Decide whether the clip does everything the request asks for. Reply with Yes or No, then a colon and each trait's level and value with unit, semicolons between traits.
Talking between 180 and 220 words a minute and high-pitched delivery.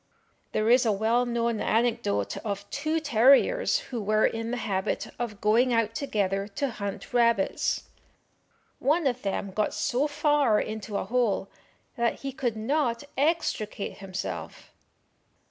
No: average, 140 wpm; high, 230 Hz